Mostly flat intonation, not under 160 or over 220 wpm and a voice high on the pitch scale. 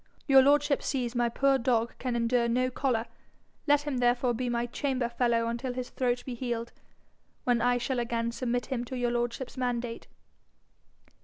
Yes: narrow, 1.5 semitones; average, 170 wpm; high, 245 Hz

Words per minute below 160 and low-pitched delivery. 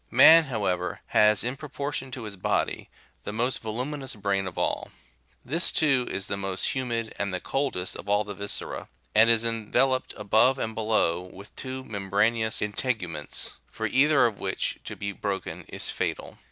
No: average, 170 wpm; low, 110 Hz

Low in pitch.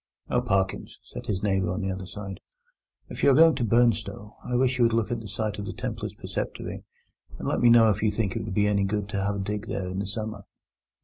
Yes: low, 105 Hz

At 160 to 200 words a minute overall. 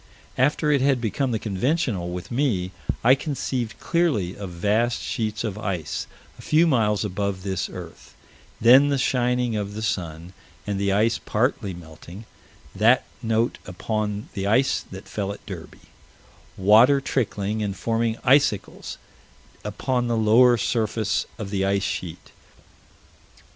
No: average, 140 wpm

